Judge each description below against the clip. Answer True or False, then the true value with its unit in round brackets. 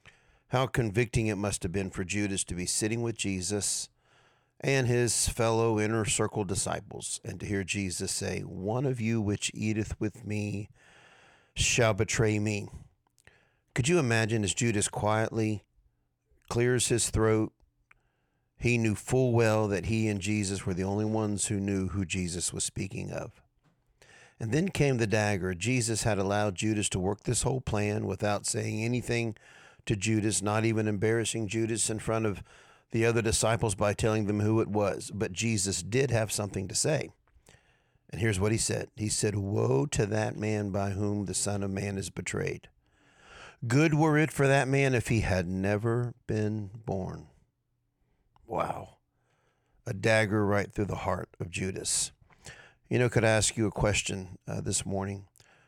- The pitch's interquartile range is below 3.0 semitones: True (2.6 semitones)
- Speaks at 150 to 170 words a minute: True (165 wpm)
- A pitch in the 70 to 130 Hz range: True (110 Hz)